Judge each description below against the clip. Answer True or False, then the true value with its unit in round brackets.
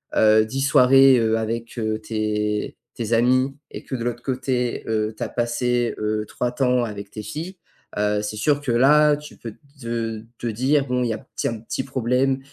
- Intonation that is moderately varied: True (3.1 semitones)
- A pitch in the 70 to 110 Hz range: False (120 Hz)